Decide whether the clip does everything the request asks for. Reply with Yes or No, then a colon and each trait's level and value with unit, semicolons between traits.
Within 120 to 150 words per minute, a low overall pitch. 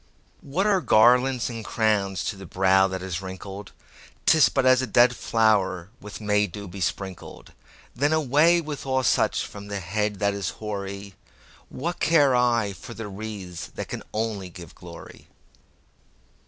Yes: average, 145 wpm; low, 105 Hz